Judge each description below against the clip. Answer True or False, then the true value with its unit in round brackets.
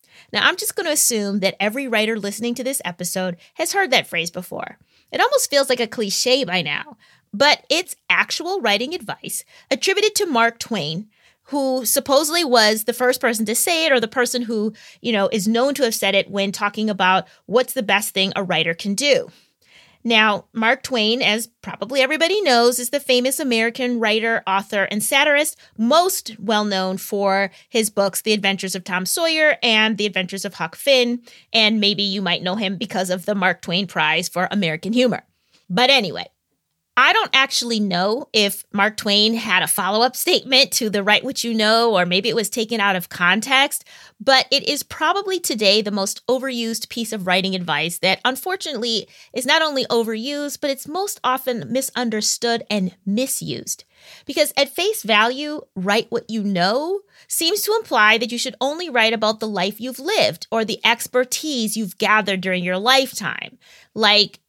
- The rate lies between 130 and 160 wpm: False (180 wpm)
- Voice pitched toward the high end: True (225 Hz)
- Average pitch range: True (4.8 semitones)